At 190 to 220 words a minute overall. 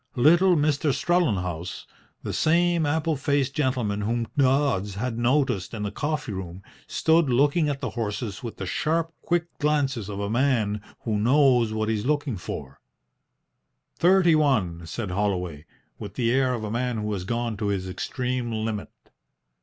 No: average, 160 wpm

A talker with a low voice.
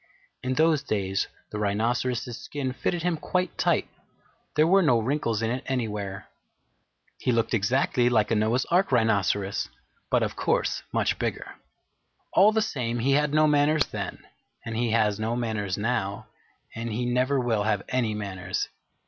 Yes: low, 120 Hz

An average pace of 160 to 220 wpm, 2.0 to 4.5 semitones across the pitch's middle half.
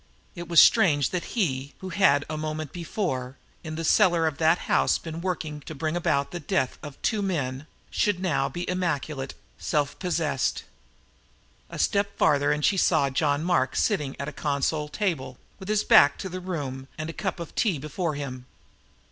Yes: average, 185 wpm; average, 4.0 semitones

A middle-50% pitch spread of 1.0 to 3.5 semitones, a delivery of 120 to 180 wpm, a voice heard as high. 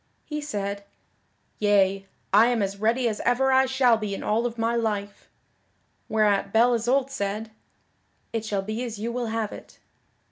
Yes: average, 2.9 semitones; average, 170 wpm; high, 225 Hz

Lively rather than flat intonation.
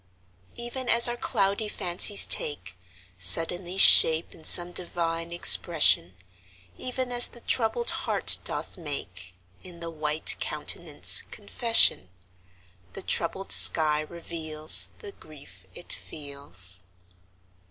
No: average, 4.7 semitones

